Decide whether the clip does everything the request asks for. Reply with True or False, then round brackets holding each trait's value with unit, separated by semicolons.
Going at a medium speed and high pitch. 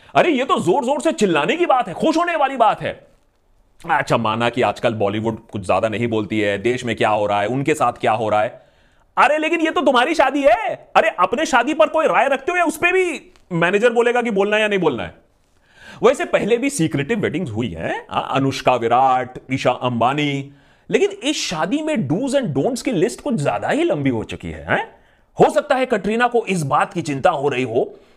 False (220 wpm; 200 Hz)